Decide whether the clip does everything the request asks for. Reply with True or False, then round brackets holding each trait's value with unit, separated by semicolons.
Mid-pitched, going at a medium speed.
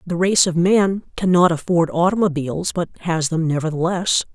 True (175 Hz; 150 wpm)